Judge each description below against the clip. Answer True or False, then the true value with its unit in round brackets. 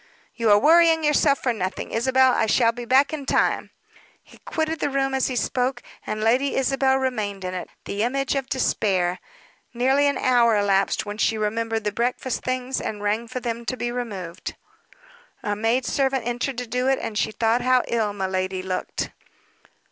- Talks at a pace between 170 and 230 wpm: True (185 wpm)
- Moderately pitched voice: False (240 Hz)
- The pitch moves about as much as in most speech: True (3.8 semitones)